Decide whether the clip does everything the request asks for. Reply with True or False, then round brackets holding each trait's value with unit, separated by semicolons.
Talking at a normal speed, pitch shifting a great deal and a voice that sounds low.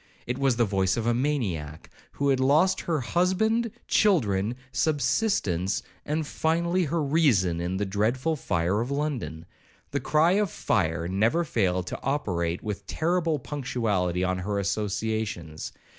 True (145 wpm; 8.4 semitones; 120 Hz)